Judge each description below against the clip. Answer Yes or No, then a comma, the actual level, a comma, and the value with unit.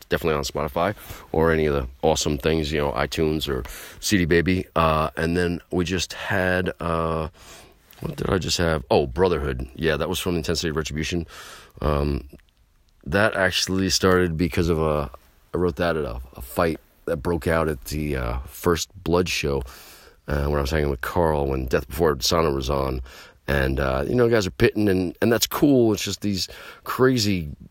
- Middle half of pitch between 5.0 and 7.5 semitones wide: No, average, 4.0 semitones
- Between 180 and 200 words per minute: Yes, average, 190 wpm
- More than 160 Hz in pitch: No, very low, 80 Hz